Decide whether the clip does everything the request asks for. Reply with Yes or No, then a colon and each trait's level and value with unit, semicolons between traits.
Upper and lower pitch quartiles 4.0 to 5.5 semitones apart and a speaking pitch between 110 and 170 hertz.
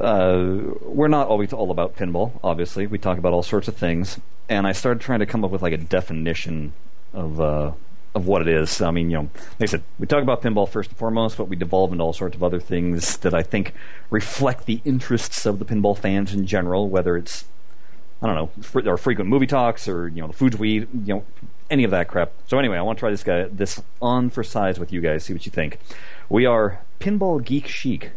No: average, 4.4 semitones; low, 100 Hz